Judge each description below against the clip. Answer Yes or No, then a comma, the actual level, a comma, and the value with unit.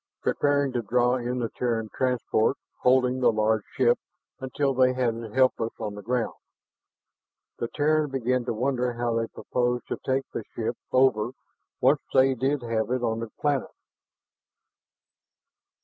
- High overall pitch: No, low, 125 Hz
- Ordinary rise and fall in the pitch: No, narrow, 2.3 semitones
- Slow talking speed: No, average, 150 wpm